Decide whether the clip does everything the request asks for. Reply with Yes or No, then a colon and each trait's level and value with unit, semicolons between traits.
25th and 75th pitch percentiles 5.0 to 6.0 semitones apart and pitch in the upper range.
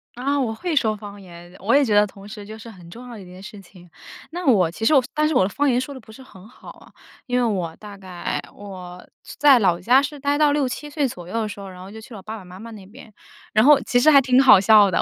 Yes: wide, 5.5 semitones; high, 220 Hz